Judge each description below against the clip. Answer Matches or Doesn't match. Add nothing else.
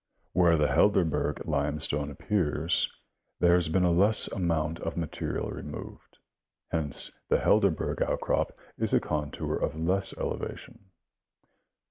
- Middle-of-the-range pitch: Doesn't match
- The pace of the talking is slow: Matches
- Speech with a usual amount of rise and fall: Matches